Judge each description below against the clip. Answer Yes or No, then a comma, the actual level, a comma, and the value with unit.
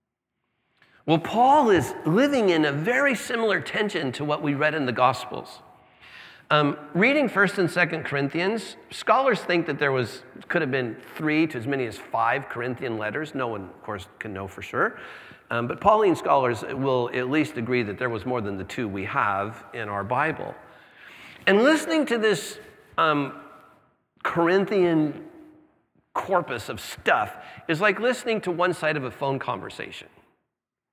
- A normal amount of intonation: No, wide, 7.7 semitones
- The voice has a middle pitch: Yes, medium, 155 Hz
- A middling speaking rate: Yes, average, 165 wpm